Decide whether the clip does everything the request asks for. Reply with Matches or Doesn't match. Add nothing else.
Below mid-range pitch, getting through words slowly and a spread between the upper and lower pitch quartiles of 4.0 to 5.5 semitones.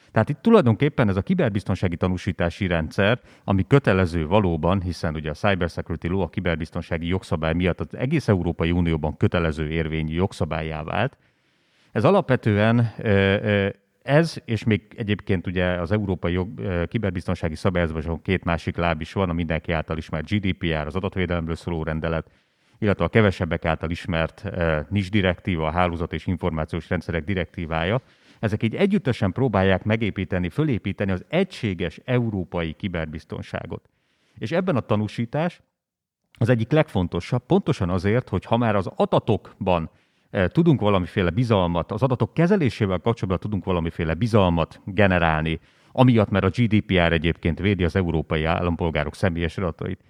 Doesn't match